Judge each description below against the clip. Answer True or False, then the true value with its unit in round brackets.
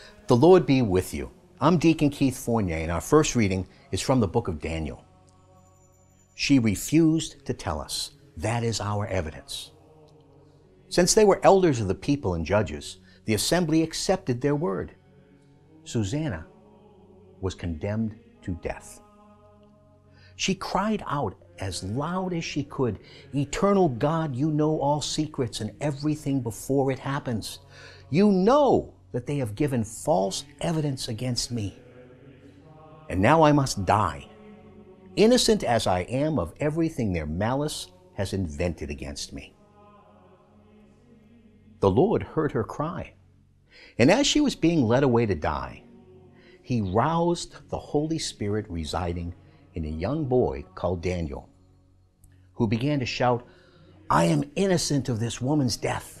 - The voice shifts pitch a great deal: True (8.0 semitones)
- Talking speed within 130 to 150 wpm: True (140 wpm)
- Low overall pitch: True (120 Hz)